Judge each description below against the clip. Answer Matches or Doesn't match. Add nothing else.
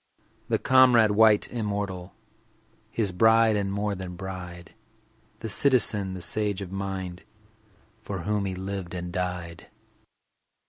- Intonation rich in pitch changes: Doesn't match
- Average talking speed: Doesn't match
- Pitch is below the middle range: Matches